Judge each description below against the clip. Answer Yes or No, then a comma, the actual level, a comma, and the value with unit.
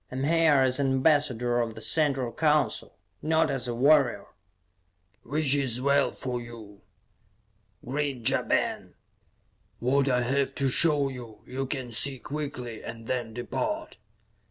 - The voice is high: No, low, 135 Hz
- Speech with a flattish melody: No, average, 3.0 semitones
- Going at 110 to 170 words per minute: Yes, average, 150 wpm